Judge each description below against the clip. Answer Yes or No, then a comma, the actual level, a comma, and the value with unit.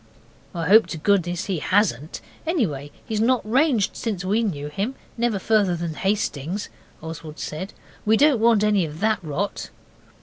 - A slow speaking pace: No, average, 160 wpm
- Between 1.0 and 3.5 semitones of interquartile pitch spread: No, average, 5.1 semitones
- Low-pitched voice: No, high, 200 Hz